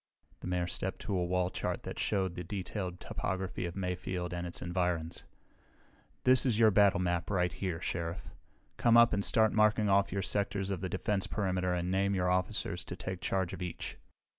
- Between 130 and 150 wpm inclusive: No, average, 190 wpm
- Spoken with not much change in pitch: Yes, narrow, 2.0 semitones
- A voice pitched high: No, very low, 95 Hz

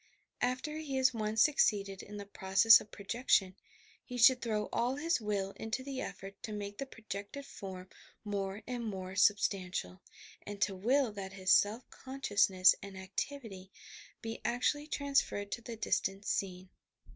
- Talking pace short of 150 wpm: No, average, 155 wpm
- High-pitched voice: Yes, high, 210 Hz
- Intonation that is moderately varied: Yes, average, 4.3 semitones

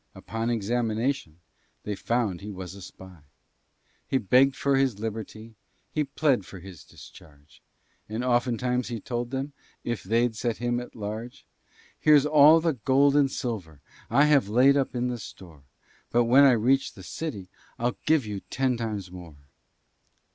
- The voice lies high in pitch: No, low, 120 Hz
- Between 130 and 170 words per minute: Yes, average, 155 wpm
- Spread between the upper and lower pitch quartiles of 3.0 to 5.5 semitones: Yes, average, 4.6 semitones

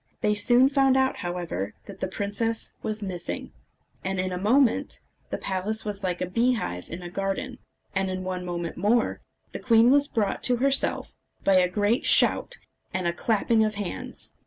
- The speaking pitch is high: Yes, high, 205 Hz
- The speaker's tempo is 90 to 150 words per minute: No, average, 180 wpm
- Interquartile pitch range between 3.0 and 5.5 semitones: Yes, average, 4.2 semitones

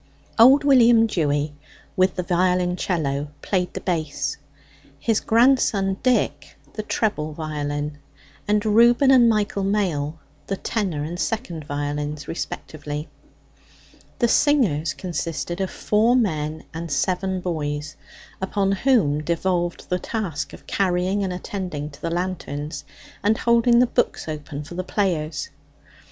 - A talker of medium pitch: Yes, medium, 180 Hz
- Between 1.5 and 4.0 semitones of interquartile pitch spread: No, wide, 5.6 semitones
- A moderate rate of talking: No, slow, 125 wpm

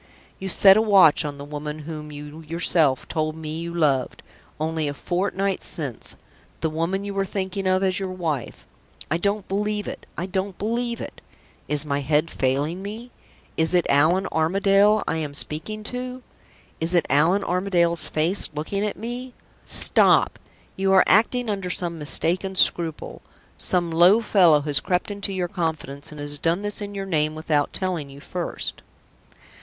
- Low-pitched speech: No, medium, 175 Hz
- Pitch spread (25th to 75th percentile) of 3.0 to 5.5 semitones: Yes, average, 4.3 semitones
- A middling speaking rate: Yes, average, 170 wpm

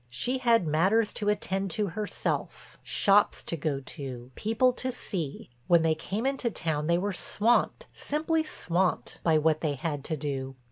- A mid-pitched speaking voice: Yes, medium, 180 Hz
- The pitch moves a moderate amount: No, wide, 6.5 semitones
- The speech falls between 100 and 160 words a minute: No, average, 170 wpm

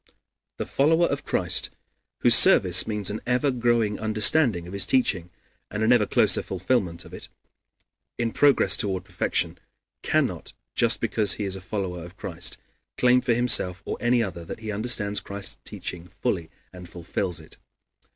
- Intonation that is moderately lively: Yes, average, 4.9 semitones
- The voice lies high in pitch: No, low, 105 Hz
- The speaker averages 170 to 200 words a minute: No, average, 160 wpm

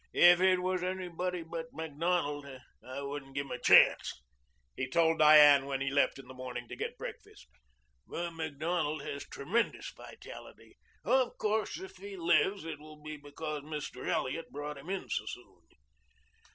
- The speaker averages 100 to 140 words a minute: No, average, 165 wpm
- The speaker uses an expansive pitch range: No, average, 4.0 semitones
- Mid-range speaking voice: Yes, medium, 155 Hz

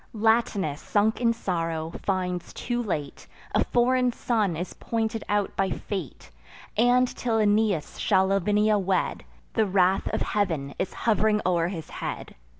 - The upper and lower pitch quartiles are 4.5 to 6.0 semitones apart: No, average, 3.7 semitones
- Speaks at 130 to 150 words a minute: Yes, average, 145 wpm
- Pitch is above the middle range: Yes, high, 205 Hz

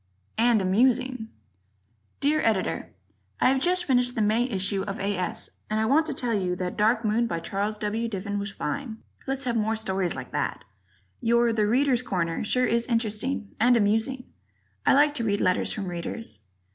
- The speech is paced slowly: No, average, 185 wpm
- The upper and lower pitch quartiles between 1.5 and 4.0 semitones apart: Yes, average, 3.7 semitones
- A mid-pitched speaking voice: No, high, 225 Hz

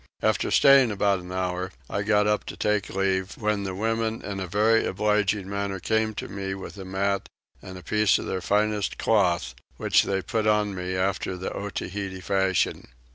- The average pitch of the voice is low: Yes, low, 100 Hz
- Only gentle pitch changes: Yes, narrow, 2.0 semitones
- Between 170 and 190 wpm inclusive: Yes, average, 185 wpm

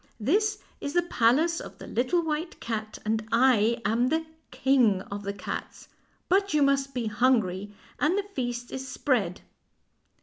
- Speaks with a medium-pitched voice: No, very high, 255 Hz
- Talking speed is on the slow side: No, average, 160 wpm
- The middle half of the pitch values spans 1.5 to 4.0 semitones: No, wide, 5.5 semitones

